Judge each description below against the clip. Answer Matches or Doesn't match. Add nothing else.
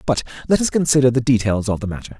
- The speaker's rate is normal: Doesn't match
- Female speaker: Doesn't match